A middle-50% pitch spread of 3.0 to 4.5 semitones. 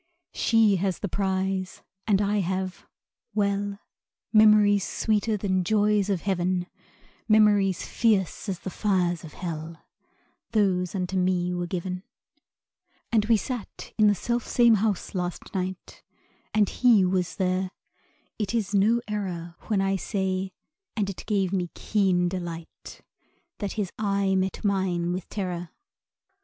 No: narrow, 2.4 semitones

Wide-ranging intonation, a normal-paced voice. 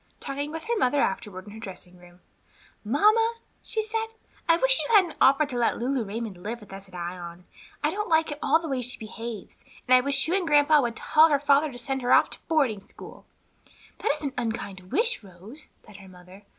No: wide, 7.3 semitones; fast, 220 wpm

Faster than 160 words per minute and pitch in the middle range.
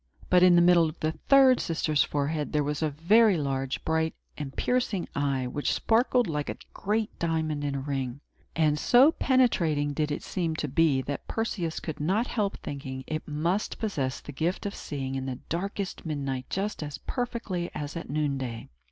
Yes: average, 185 wpm; medium, 155 Hz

